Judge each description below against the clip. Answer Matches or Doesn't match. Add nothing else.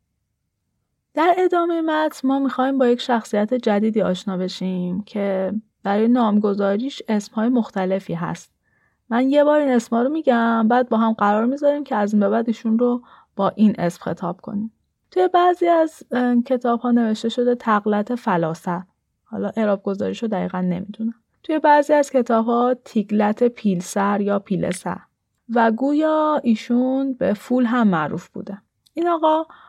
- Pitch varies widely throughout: Doesn't match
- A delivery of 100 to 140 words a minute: Doesn't match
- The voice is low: Doesn't match